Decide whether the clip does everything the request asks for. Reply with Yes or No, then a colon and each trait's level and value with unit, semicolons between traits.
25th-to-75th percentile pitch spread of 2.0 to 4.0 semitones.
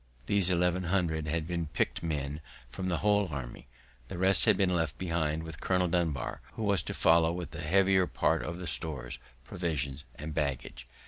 Yes: average, 3.2 semitones